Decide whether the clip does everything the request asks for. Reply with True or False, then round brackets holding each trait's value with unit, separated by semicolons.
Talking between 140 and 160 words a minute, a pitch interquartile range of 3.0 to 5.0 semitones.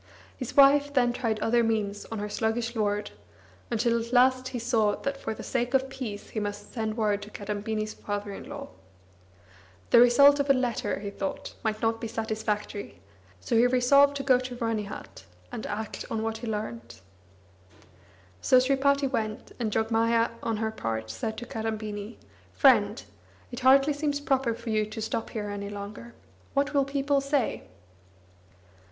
False (170 wpm; 3.3 semitones)